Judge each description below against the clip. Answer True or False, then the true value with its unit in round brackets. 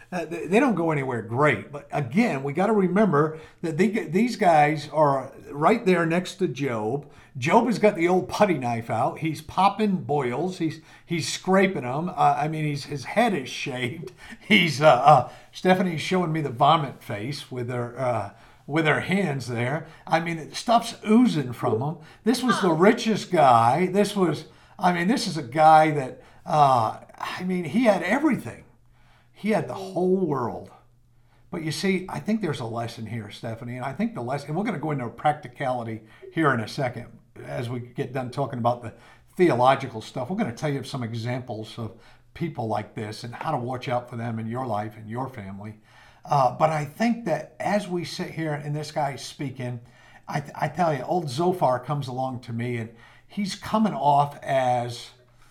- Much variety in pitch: True (6.7 semitones)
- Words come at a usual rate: True (195 wpm)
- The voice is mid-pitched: True (145 Hz)